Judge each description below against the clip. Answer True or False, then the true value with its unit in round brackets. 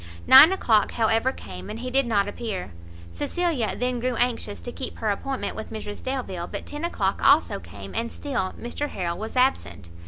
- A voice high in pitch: True (235 Hz)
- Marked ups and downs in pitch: False (4.3 semitones)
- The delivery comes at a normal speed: True (185 wpm)